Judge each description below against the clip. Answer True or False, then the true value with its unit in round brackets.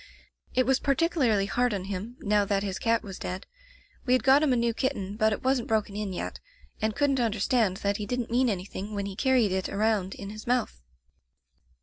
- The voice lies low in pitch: False (215 Hz)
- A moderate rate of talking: False (210 wpm)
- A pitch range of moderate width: True (3.8 semitones)